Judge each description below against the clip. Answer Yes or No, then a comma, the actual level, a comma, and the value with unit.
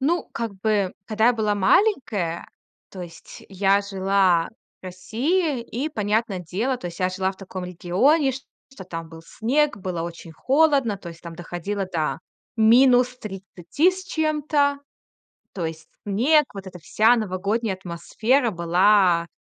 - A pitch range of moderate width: No, wide, 5.9 semitones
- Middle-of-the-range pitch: No, high, 200 Hz